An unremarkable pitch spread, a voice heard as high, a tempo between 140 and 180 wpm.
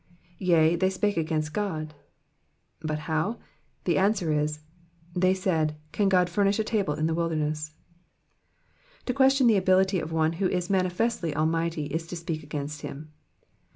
No: average, 3.4 semitones; medium, 170 Hz; average, 165 wpm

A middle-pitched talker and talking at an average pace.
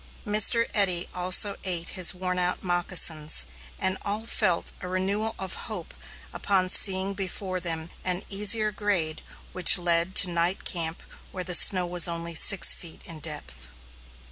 Yes: medium, 180 Hz; average, 150 wpm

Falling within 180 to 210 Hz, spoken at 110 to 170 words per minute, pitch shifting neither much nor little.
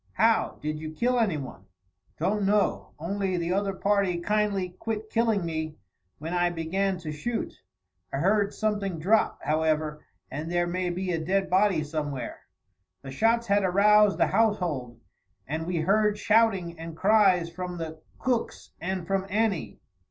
Yes: medium, 185 Hz; average, 150 wpm; average, 4.4 semitones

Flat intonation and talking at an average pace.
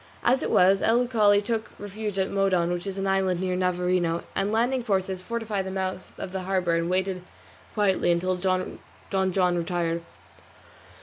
Yes: narrow, 2.0 semitones; average, 170 wpm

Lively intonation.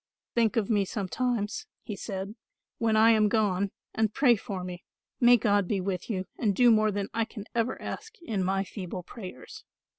No: average, 2.9 semitones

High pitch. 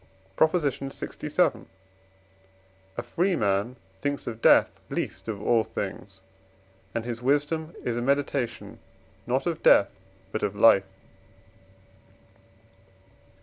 No: low, 120 Hz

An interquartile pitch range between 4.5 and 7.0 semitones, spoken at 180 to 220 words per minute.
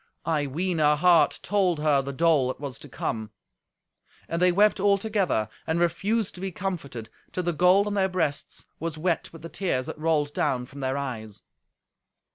Yes: average, 4.8 semitones; average, 190 wpm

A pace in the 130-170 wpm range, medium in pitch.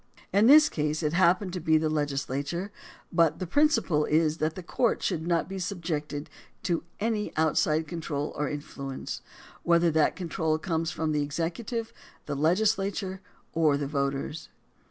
Yes: average, 155 wpm; medium, 160 Hz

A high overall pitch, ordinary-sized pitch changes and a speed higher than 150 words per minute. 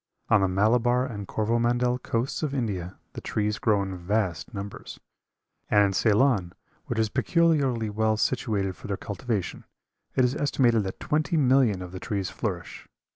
No: low, 110 Hz; average, 4.0 semitones; average, 160 wpm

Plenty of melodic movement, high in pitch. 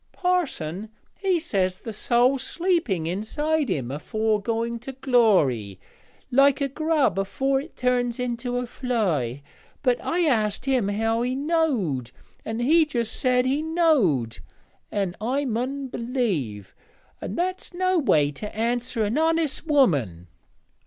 Yes: wide, 5.9 semitones; high, 245 Hz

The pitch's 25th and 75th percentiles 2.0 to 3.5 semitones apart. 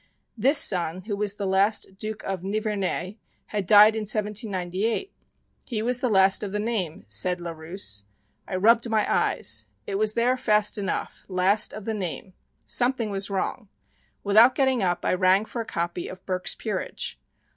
Yes: average, 2.8 semitones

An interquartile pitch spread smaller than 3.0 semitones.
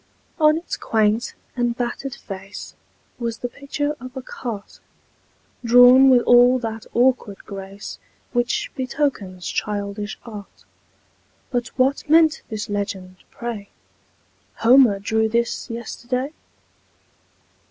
No: average, 3.7 semitones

